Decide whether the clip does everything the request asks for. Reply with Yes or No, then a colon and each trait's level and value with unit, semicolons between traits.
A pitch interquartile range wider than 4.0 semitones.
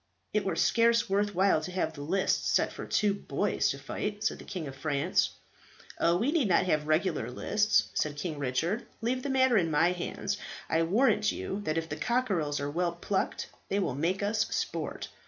Yes: average, 5.2 semitones